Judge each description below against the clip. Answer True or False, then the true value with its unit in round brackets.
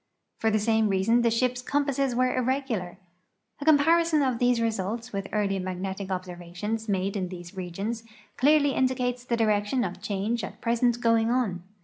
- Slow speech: False (160 wpm)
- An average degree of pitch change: True (4.4 semitones)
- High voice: True (225 Hz)